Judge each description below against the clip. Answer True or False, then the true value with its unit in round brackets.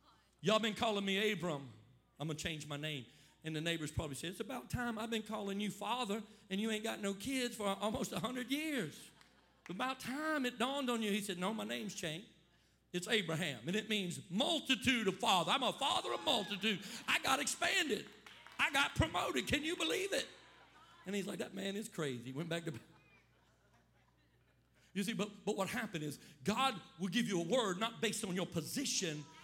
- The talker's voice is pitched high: True (205 Hz)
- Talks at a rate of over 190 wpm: True (200 wpm)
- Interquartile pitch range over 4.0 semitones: True (5.2 semitones)